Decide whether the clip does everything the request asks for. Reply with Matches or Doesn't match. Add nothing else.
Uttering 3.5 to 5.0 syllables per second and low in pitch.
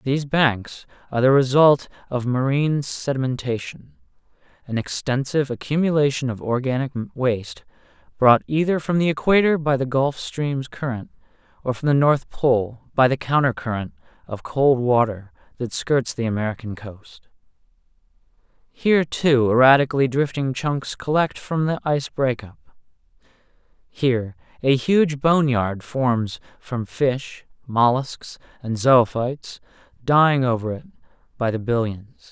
Matches